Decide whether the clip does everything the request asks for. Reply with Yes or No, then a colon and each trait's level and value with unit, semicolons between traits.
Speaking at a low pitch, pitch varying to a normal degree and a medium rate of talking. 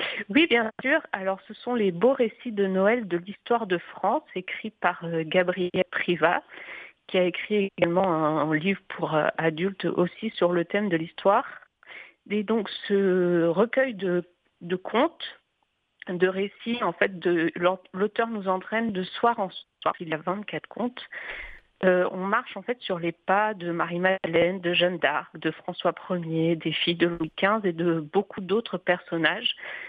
No: medium, 185 Hz; average, 3.5 semitones; average, 165 wpm